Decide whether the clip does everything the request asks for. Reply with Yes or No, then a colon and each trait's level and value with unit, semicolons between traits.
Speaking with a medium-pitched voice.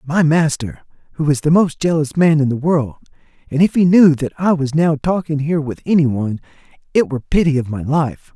Yes: medium, 150 Hz